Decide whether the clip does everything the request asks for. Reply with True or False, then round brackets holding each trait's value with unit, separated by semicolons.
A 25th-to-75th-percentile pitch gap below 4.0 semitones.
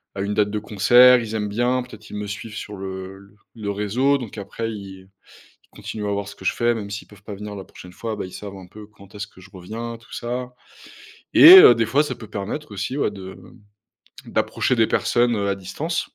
True (2.9 semitones)